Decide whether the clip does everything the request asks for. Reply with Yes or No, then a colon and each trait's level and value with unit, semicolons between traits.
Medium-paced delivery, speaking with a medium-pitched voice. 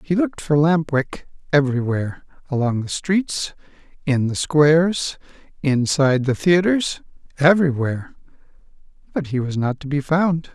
No: slow, 130 wpm; medium, 150 Hz